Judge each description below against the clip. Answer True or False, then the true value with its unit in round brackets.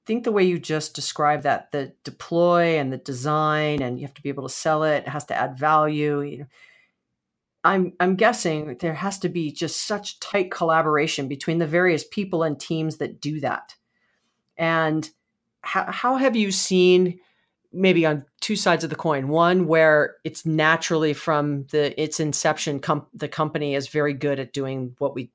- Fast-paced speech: False (185 wpm)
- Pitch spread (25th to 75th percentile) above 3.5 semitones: False (2.9 semitones)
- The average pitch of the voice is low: False (155 Hz)